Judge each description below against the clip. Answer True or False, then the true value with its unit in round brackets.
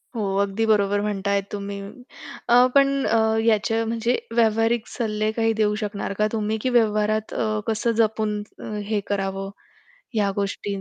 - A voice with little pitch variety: True (1.8 semitones)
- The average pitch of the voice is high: True (215 Hz)